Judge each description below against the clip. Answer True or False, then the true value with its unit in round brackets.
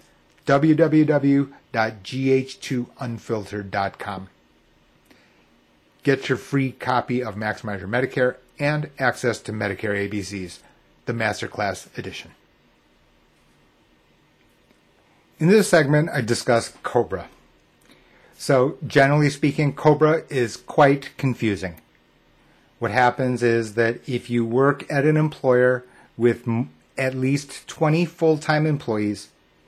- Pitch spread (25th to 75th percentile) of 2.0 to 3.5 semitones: False (4.9 semitones)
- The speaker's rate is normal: False (95 wpm)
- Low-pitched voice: True (125 Hz)